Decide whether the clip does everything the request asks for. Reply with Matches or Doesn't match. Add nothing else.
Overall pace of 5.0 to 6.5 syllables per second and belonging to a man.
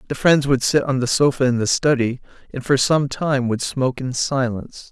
Matches